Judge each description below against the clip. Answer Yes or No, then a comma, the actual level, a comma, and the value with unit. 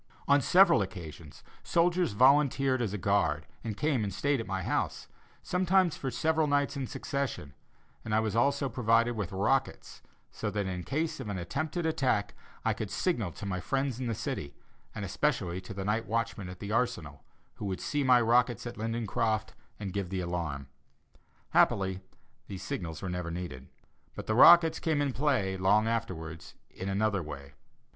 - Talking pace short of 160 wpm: No, average, 175 wpm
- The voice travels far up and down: Yes, wide, 6.4 semitones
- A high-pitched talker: No, low, 110 Hz